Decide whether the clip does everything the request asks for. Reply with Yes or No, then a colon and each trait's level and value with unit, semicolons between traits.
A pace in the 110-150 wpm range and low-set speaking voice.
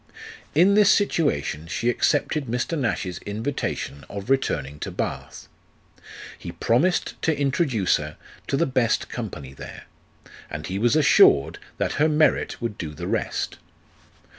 Yes: average, 140 wpm; low, 120 Hz